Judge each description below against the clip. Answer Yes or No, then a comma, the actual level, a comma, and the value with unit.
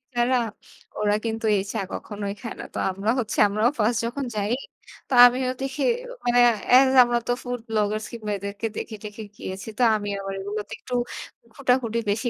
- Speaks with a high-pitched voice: Yes, high, 225 Hz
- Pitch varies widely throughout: No, average, 2.9 semitones